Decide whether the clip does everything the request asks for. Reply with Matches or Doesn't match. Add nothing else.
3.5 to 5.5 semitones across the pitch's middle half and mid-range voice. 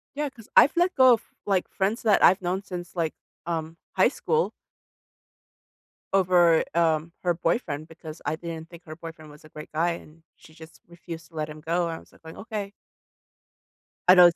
Doesn't match